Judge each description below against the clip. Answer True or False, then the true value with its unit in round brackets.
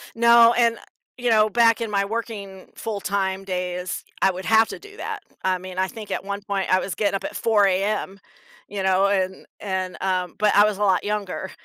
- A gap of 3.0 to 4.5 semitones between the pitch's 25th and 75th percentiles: False (2.5 semitones)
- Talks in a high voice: True (200 Hz)